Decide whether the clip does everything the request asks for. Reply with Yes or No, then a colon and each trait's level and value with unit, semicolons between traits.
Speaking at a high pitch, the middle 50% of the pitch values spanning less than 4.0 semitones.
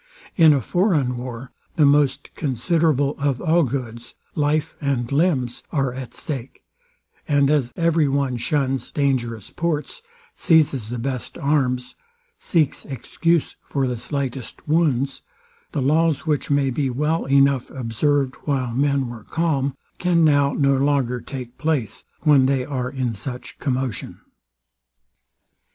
No: medium, 140 Hz; average, 3.0 semitones